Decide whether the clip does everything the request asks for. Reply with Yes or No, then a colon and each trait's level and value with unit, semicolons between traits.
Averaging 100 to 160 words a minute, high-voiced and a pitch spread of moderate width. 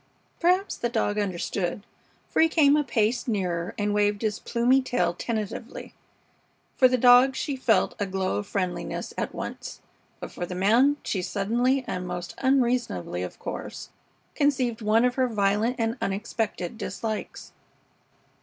Yes: average, 150 wpm; high, 225 Hz; average, 4.2 semitones